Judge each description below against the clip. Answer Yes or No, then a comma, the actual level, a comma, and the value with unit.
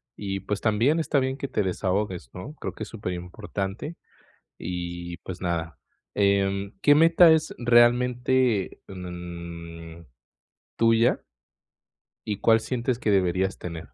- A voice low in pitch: Yes, low, 100 Hz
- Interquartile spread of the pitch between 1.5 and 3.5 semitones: No, wide, 5.4 semitones